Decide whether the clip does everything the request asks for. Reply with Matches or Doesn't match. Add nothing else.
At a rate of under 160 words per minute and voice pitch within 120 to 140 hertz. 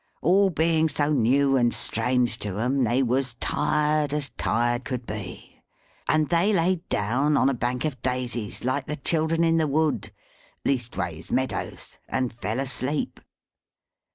Matches